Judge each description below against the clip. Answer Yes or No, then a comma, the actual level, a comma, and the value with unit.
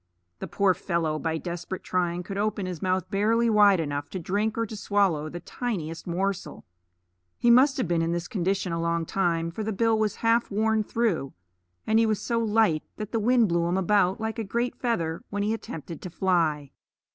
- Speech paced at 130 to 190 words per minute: No, fast, 205 wpm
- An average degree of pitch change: Yes, average, 4.5 semitones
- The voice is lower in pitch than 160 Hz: No, high, 195 Hz